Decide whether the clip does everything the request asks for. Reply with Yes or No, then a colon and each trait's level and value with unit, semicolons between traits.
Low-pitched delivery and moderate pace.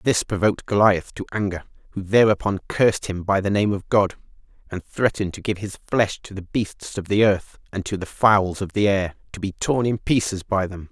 No: low, 100 Hz; fast, 220 wpm